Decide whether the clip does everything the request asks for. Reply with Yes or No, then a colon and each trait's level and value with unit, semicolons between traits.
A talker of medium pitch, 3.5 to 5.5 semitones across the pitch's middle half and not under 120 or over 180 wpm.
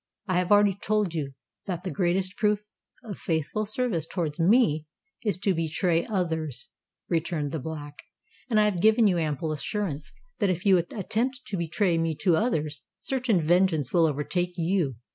Yes: medium, 175 Hz; average, 4.3 semitones; average, 165 wpm